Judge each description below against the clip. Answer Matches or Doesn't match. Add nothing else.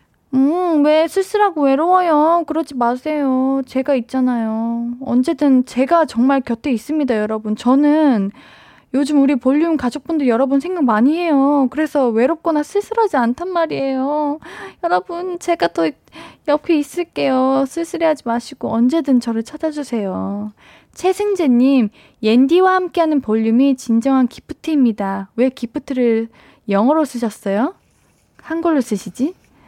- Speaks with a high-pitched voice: Matches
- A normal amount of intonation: Matches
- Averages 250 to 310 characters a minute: Matches